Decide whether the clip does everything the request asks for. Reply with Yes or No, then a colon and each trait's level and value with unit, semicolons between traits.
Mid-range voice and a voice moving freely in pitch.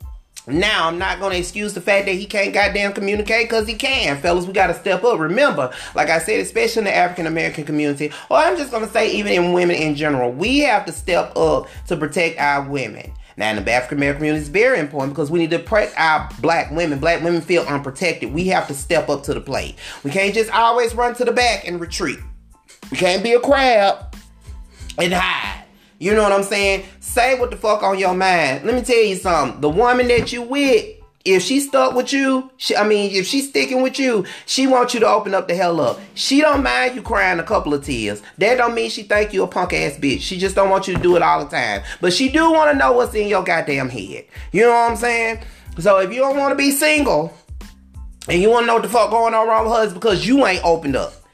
No: high, 200 Hz; wide, 6.2 semitones